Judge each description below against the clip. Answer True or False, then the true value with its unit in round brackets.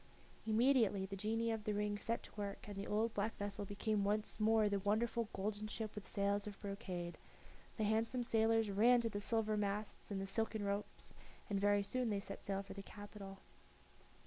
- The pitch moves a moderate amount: False (1.8 semitones)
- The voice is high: True (210 Hz)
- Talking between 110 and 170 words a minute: False (195 wpm)